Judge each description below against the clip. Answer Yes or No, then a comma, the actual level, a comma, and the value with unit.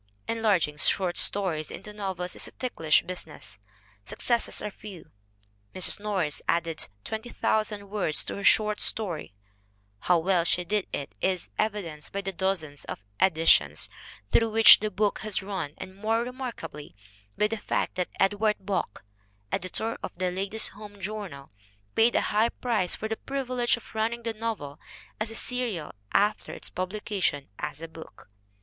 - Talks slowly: No, average, 160 wpm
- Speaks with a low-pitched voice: No, high, 200 Hz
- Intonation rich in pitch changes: No, average, 4.4 semitones